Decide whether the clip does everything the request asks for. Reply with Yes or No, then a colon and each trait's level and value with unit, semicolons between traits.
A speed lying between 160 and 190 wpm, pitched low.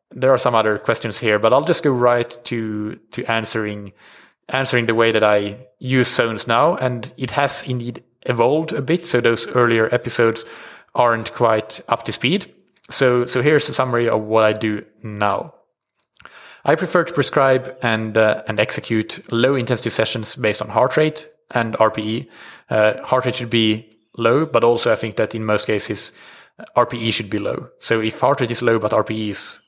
Yes: average, 185 wpm; low, 115 Hz